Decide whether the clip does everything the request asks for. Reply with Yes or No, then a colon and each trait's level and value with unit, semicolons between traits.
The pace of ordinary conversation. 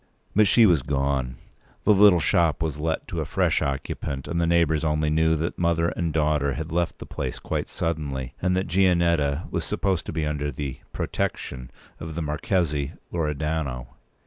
Yes: average, 175 wpm